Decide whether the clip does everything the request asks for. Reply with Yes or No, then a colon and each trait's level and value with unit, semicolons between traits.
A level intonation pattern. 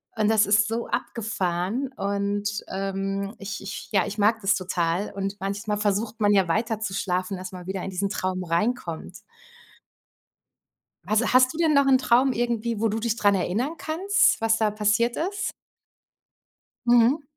No: average, 3.1 semitones